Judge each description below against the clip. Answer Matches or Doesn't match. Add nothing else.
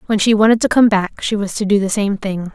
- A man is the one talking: Doesn't match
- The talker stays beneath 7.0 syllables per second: Matches